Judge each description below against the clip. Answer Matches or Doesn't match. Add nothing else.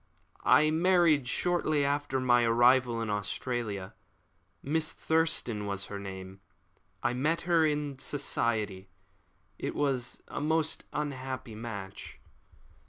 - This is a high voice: Doesn't match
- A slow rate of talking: Matches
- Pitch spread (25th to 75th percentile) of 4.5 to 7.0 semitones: Matches